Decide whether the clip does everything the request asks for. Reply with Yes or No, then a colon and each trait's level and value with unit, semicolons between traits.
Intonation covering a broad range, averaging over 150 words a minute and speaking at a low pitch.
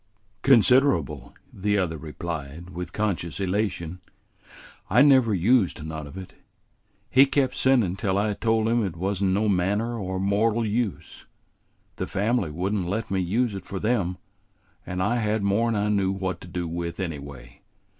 No: average, 4.0 semitones; average, 165 wpm; very low, 95 Hz